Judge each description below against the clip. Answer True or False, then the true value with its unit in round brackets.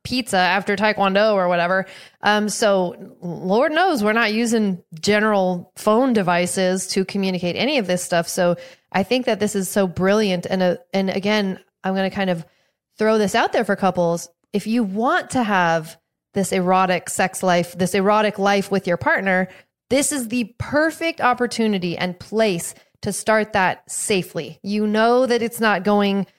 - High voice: True (195 Hz)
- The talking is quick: False (175 wpm)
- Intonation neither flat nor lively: True (3.1 semitones)